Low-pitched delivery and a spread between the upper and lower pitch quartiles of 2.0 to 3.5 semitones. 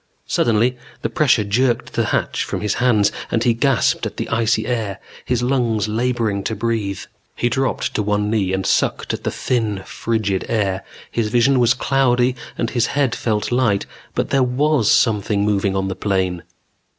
Yes: low, 115 Hz; average, 3.2 semitones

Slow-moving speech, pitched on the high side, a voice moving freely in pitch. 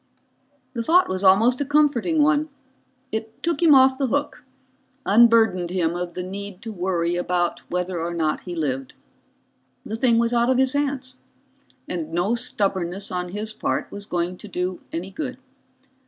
No: average, 170 wpm; high, 205 Hz; wide, 6.1 semitones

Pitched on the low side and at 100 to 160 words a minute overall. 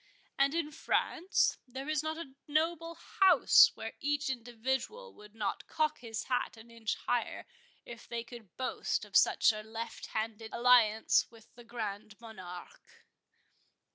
No: high, 240 Hz; average, 145 wpm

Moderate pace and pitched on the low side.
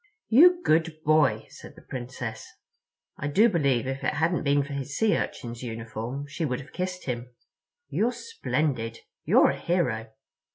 No: average, 160 wpm; medium, 145 Hz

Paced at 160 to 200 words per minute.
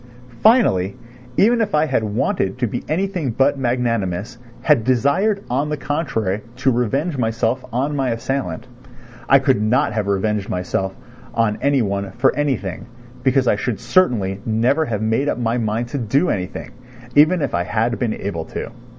Yes: average, 170 wpm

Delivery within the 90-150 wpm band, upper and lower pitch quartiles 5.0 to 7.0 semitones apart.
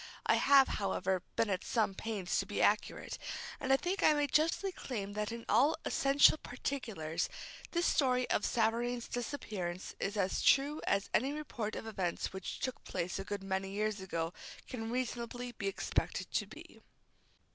No: average, 170 wpm; average, 5.3 semitones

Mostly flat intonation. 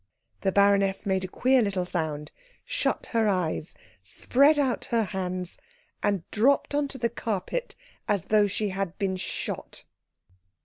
No: average, 4.0 semitones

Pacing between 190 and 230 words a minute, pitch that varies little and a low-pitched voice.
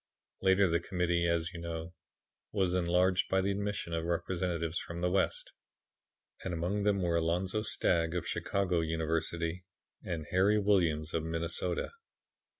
No: average, 145 wpm; narrow, 2.2 semitones; very low, 85 Hz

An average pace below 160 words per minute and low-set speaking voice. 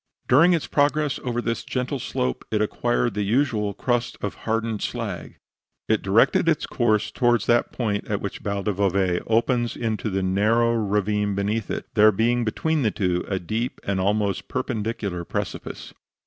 No: average, 165 wpm; low, 110 Hz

